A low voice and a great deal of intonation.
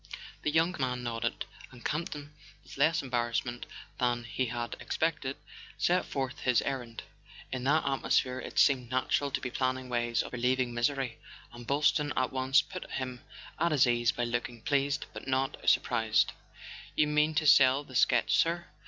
No: low, 130 Hz; average, 3.0 semitones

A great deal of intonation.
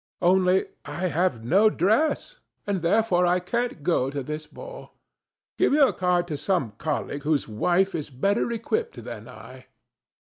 Yes: wide, 6.0 semitones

